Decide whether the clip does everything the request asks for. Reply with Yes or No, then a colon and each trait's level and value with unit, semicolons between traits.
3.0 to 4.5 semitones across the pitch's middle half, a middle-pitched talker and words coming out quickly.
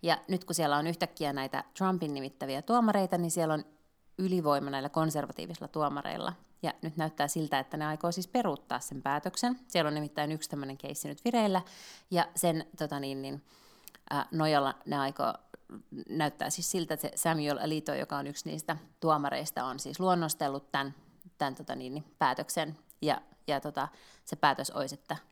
Yes: average, 3.3 semitones; medium, 155 Hz; fast, 170 wpm